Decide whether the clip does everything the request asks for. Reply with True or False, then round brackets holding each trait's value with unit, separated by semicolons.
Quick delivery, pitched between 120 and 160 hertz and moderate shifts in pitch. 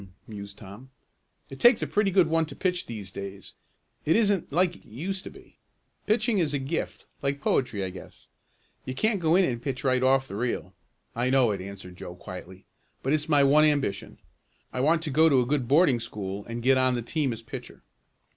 False (210 wpm; 135 Hz; 6.5 semitones)